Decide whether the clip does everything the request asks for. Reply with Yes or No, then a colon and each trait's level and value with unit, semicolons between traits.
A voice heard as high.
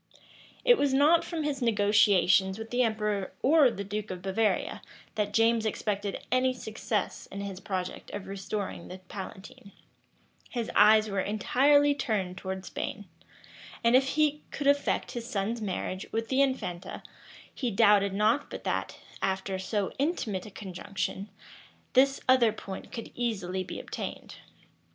Yes: high, 215 Hz